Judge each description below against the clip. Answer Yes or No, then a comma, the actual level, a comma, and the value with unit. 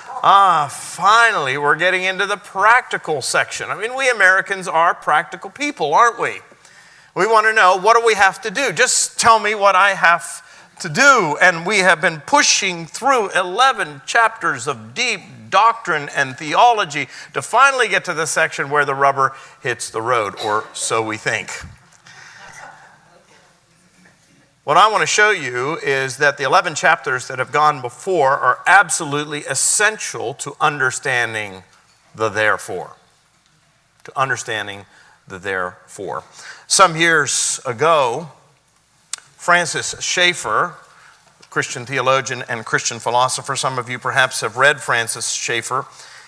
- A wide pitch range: Yes, wide, 6.9 semitones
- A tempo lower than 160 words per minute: Yes, average, 140 wpm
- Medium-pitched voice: Yes, medium, 175 Hz